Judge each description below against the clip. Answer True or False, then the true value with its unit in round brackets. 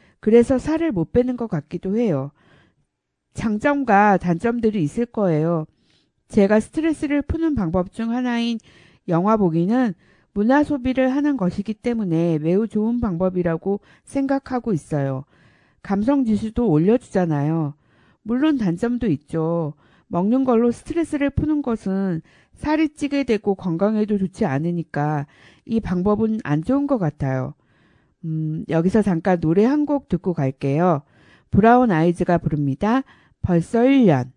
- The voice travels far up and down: True (6.6 semitones)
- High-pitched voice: True (200 Hz)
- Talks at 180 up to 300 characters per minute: True (285 characters per minute)